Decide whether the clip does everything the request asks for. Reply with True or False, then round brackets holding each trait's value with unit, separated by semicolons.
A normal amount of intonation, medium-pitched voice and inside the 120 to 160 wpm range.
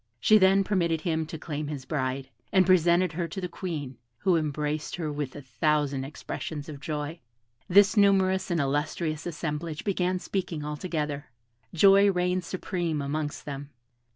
True (3.7 semitones; 160 Hz; 155 wpm)